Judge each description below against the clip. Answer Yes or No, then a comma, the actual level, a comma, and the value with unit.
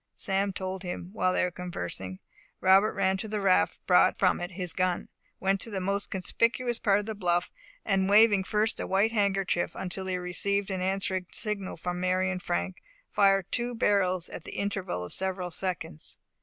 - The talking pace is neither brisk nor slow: Yes, average, 190 wpm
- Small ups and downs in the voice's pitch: Yes, narrow, 1.8 semitones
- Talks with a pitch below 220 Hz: Yes, high, 190 Hz